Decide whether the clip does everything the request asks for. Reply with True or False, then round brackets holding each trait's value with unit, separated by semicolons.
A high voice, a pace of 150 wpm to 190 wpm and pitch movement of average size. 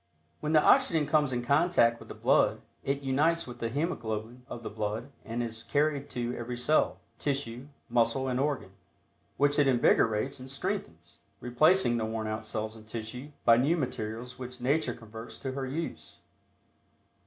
False (125 Hz; 165 wpm; 3.6 semitones)